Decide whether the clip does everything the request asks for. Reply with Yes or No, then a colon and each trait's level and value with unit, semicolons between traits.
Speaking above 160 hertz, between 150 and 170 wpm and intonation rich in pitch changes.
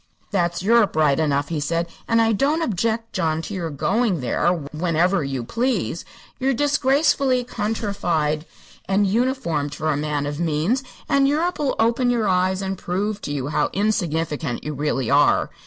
Yes: medium, 185 Hz; average, 160 wpm; wide, 7.3 semitones